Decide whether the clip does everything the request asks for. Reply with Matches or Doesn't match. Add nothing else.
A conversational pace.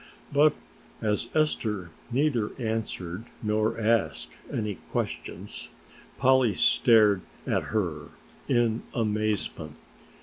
Doesn't match